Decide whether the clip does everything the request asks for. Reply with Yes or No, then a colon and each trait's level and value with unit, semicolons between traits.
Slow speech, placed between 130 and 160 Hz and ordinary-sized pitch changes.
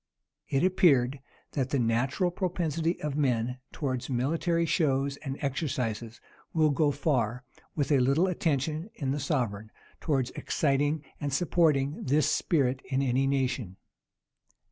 Yes: slow, 130 wpm; medium, 140 Hz; average, 3.3 semitones